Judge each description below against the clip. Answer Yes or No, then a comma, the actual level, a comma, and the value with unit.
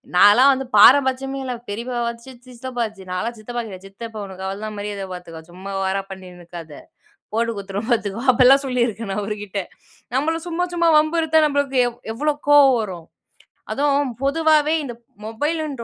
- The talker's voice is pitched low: No, high, 235 Hz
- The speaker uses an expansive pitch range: Yes, wide, 5.7 semitones